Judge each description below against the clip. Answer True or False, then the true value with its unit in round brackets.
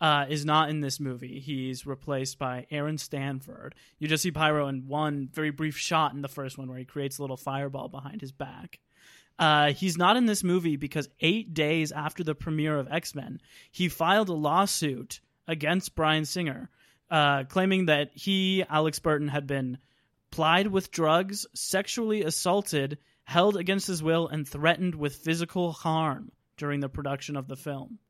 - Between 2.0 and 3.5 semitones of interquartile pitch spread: True (3.1 semitones)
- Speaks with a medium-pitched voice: True (150 Hz)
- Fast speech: False (175 wpm)